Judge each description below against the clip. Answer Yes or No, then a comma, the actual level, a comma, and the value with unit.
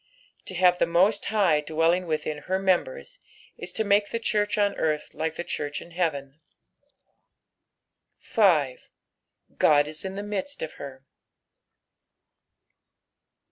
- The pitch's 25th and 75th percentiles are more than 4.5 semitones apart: Yes, average, 4.9 semitones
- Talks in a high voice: No, medium, 175 Hz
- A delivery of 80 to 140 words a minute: Yes, slow, 135 wpm